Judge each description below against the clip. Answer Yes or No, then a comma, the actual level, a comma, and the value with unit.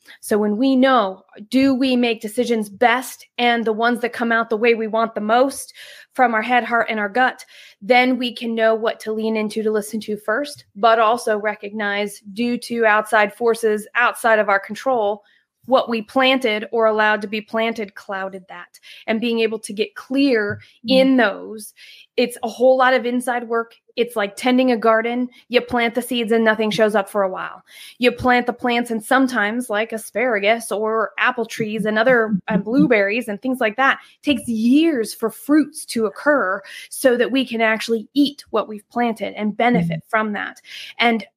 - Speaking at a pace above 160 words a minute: Yes, average, 190 wpm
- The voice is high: Yes, high, 230 Hz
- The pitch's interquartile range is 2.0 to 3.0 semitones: Yes, narrow, 2.4 semitones